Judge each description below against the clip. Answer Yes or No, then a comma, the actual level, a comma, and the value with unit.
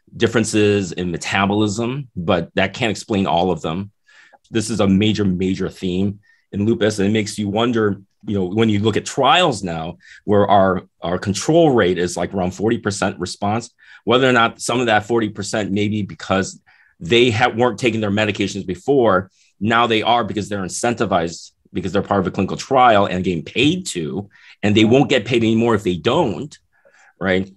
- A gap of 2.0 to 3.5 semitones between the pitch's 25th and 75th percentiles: Yes, average, 3.1 semitones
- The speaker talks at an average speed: Yes, average, 185 wpm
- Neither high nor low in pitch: No, low, 105 Hz